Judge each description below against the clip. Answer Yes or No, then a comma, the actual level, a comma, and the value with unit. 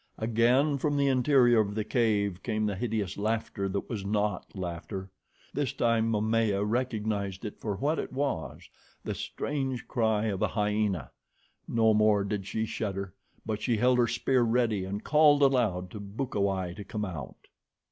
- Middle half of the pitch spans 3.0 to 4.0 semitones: Yes, average, 3.3 semitones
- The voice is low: Yes, low, 110 Hz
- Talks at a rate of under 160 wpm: No, average, 165 wpm